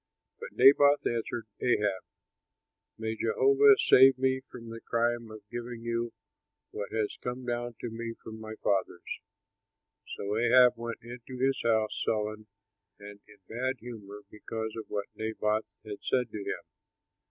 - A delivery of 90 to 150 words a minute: Yes, average, 145 wpm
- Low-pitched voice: Yes, low, 115 Hz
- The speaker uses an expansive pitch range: No, narrow, 2.4 semitones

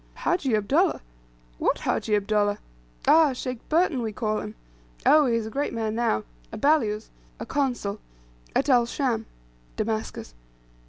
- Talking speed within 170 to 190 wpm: No, average, 145 wpm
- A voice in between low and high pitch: No, high, 230 Hz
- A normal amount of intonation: Yes, average, 4.6 semitones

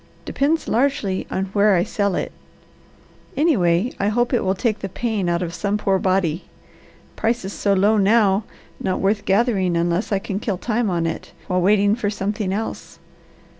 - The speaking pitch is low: No, high, 200 Hz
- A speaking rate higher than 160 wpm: Yes, average, 170 wpm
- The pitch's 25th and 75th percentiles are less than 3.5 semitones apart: Yes, average, 2.8 semitones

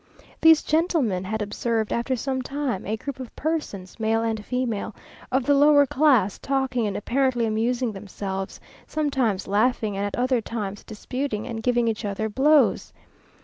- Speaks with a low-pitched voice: No, high, 235 Hz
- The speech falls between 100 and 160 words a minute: Yes, average, 155 wpm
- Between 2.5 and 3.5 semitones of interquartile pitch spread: No, average, 4.3 semitones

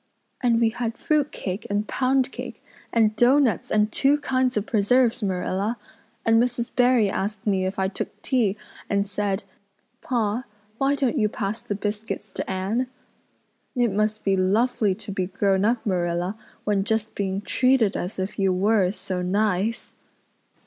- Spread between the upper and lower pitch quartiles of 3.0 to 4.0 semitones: Yes, average, 3.7 semitones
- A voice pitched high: Yes, high, 215 Hz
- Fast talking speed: No, average, 165 wpm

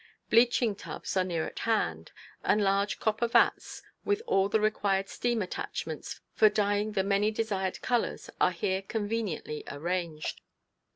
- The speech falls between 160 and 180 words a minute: No, average, 140 wpm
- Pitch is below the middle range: No, high, 205 Hz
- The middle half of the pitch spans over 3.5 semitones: No, average, 2.7 semitones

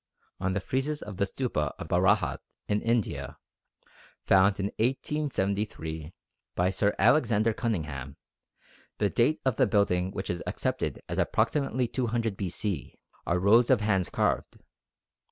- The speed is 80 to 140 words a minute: Yes, slow, 135 wpm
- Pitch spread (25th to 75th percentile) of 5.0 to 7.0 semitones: No, average, 4.0 semitones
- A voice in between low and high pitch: No, low, 105 Hz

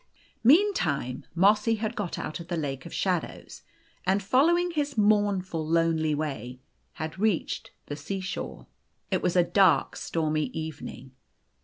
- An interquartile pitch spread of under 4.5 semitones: No, average, 5.1 semitones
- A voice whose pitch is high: No, medium, 180 Hz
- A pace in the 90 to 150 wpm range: Yes, average, 145 wpm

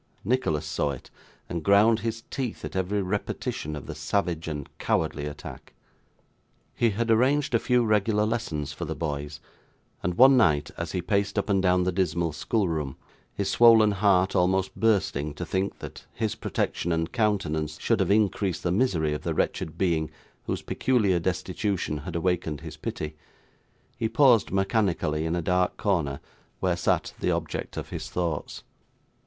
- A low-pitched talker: Yes, very low, 90 Hz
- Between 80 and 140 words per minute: No, average, 165 wpm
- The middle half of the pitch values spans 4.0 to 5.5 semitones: Yes, average, 5.1 semitones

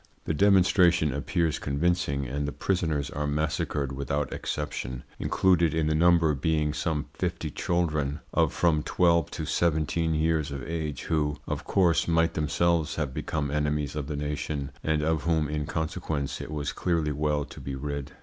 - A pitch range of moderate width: No, narrow, 2.2 semitones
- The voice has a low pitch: Yes, very low, 75 Hz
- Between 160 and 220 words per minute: Yes, average, 165 wpm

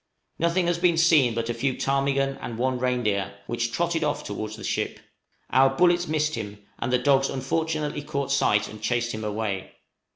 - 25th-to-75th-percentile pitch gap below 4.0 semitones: No, average, 4.9 semitones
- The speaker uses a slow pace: No, average, 185 wpm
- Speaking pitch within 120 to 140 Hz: Yes, low, 135 Hz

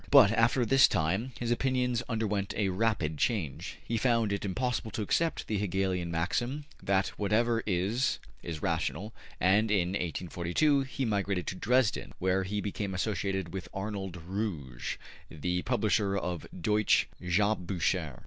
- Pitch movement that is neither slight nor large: Yes, average, 4.0 semitones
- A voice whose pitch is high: No, low, 100 Hz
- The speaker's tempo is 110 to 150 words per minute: Yes, average, 140 wpm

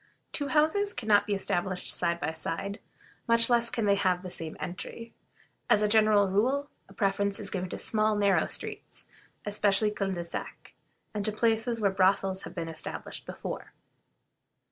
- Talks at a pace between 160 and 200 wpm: Yes, average, 170 wpm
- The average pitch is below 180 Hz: No, high, 205 Hz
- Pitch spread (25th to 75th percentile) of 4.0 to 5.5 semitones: No, average, 2.9 semitones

